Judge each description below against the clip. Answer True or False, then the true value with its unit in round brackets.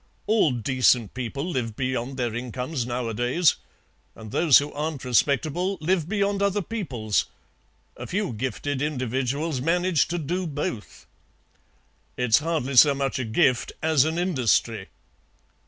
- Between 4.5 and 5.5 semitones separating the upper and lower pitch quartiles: True (5.2 semitones)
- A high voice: False (140 Hz)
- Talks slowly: True (130 wpm)